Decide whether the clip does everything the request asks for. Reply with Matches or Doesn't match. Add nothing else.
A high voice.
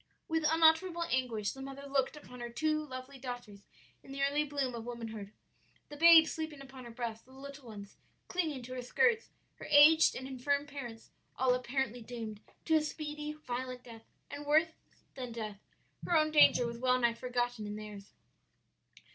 Matches